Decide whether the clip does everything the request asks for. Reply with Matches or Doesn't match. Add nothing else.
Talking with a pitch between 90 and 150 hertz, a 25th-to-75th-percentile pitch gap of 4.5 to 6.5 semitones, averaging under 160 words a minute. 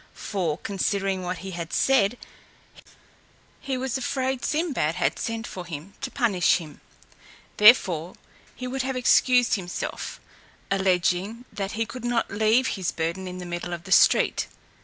Doesn't match